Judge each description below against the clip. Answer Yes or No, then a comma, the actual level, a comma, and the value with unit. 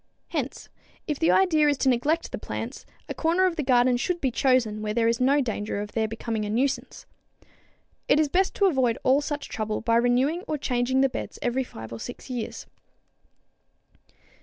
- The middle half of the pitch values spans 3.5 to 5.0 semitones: Yes, average, 4.2 semitones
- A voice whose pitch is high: Yes, very high, 255 Hz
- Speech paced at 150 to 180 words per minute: No, average, 190 wpm